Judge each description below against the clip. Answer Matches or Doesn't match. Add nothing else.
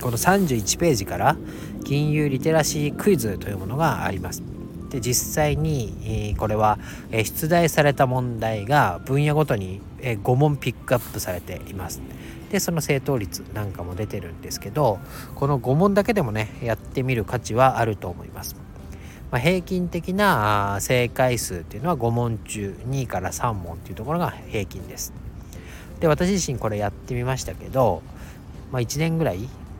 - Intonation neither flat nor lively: Doesn't match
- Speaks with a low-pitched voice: Matches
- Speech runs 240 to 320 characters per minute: Matches